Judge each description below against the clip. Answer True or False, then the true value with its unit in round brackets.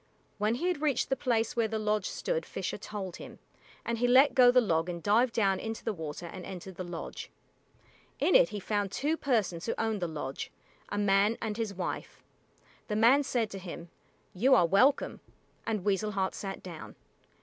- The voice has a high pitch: True (210 Hz)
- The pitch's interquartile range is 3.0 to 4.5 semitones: True (4.2 semitones)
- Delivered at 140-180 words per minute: False (195 wpm)